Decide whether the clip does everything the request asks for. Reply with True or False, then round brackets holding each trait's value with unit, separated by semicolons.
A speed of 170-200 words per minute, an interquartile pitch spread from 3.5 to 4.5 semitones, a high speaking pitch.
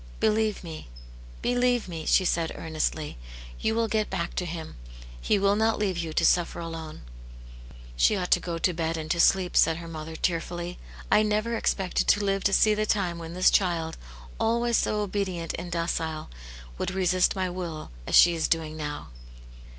False (190 wpm; 3.8 semitones; 175 Hz)